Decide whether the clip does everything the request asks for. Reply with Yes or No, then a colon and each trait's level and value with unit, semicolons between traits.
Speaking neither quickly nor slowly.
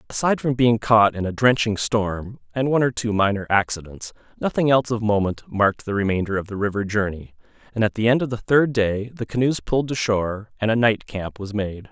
No: fast, 220 wpm